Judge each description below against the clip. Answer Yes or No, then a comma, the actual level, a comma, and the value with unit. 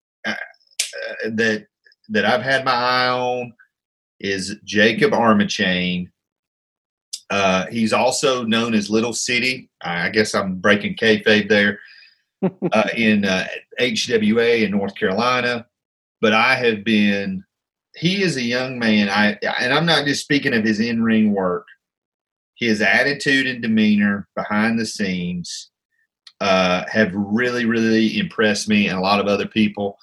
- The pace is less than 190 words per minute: Yes, average, 140 wpm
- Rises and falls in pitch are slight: No, average, 3.3 semitones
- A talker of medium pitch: No, low, 110 Hz